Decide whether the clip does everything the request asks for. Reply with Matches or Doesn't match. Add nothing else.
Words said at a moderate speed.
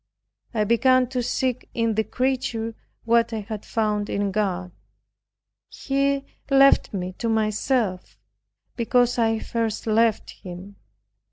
Doesn't match